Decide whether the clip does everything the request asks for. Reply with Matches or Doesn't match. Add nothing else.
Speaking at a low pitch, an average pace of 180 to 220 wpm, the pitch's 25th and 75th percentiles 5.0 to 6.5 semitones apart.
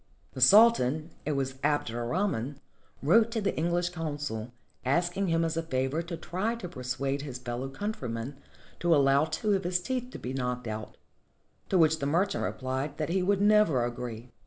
Doesn't match